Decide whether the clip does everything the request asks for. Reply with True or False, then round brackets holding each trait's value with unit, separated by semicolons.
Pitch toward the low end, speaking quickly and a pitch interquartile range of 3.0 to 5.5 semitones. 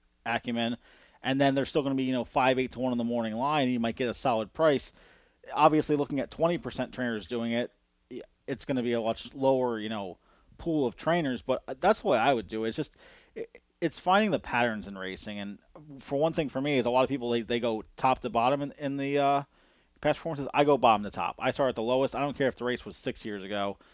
True (125 Hz; 255 wpm; 3.6 semitones)